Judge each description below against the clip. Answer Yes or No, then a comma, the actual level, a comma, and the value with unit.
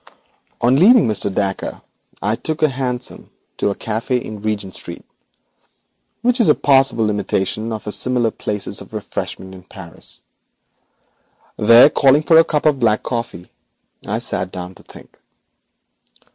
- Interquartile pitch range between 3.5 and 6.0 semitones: Yes, average, 5.0 semitones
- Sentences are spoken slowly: No, average, 145 wpm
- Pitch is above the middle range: No, low, 115 Hz